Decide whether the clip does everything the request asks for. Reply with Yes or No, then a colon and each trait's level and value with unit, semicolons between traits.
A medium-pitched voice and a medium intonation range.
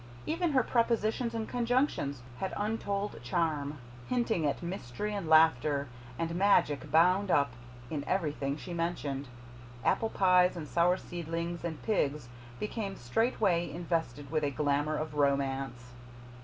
No: medium, 170 Hz; wide, 5.8 semitones